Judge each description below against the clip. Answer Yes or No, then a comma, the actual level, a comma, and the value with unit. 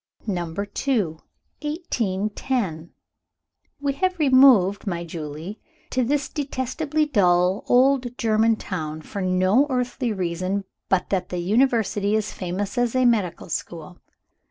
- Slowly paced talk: Yes, slow, 120 wpm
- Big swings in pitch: Yes, wide, 6.1 semitones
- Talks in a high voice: Yes, high, 210 Hz